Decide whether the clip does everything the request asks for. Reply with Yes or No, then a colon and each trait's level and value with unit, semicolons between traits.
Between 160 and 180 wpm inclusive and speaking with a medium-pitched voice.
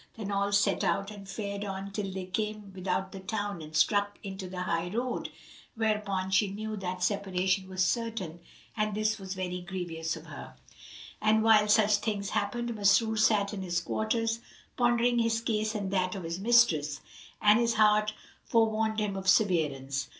No: average, 170 wpm; high, 200 Hz